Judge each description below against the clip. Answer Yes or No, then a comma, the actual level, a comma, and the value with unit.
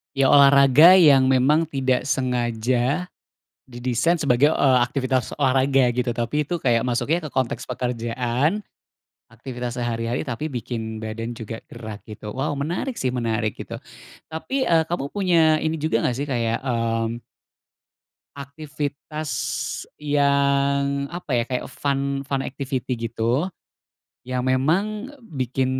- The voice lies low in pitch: Yes, low, 130 Hz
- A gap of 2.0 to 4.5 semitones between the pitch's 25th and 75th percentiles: Yes, average, 3.4 semitones